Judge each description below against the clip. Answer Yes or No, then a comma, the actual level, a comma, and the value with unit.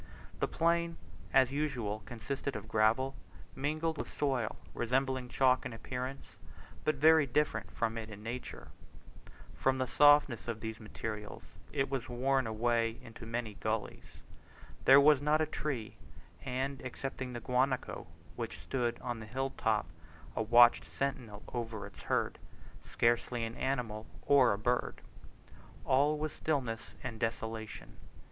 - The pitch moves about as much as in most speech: Yes, average, 3.4 semitones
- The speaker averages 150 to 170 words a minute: No, average, 140 wpm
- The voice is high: No, low, 125 Hz